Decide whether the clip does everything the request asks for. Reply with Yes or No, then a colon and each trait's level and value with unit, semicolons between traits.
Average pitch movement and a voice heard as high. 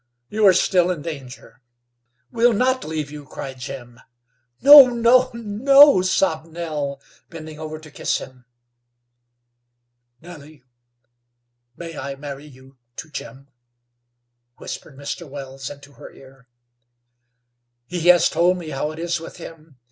No: average, 4.6 semitones; medium, 155 Hz